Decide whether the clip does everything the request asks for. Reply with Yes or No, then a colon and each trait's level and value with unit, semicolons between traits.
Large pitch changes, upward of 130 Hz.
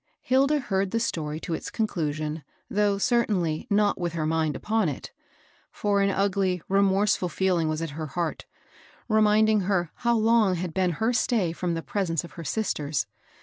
No: average, 4.4 semitones; high, 190 Hz